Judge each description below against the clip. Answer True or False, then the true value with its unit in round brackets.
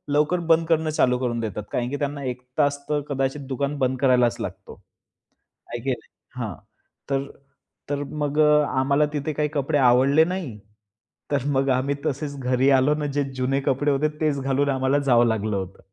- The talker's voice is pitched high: False (135 Hz)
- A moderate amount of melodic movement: False (2.3 semitones)